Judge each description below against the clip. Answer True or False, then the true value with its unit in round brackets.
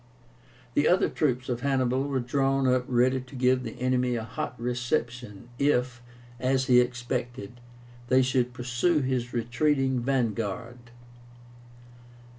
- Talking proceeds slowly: True (125 wpm)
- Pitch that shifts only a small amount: True (1.5 semitones)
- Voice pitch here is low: True (125 Hz)